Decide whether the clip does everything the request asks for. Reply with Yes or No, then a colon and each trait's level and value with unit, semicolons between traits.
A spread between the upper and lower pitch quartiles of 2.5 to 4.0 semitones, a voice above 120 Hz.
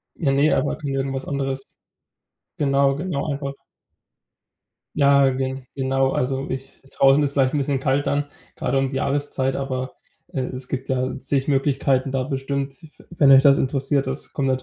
No: narrow, 0.9 semitones; low, 135 Hz